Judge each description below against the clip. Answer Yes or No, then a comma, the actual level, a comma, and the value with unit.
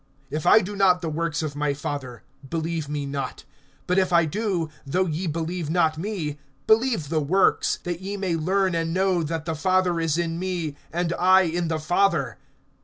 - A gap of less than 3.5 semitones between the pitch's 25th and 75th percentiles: Yes, average, 3.1 semitones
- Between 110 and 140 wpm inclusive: No, average, 190 wpm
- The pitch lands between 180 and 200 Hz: No, medium, 170 Hz